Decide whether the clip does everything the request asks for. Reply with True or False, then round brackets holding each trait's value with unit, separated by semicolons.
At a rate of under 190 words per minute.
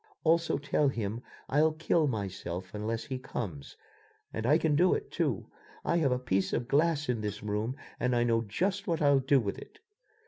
False (195 wpm)